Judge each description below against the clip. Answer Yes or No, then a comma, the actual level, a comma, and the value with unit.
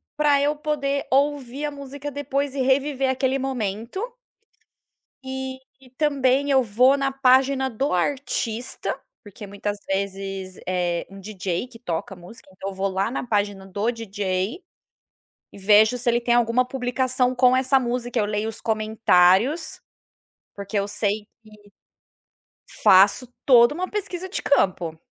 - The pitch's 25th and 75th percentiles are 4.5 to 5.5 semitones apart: Yes, average, 5.1 semitones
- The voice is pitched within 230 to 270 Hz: Yes, high, 245 Hz